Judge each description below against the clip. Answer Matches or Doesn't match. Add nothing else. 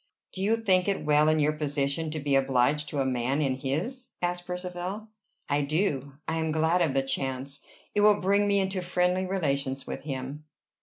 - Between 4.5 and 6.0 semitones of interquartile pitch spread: Matches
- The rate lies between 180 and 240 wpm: Matches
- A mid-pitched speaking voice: Matches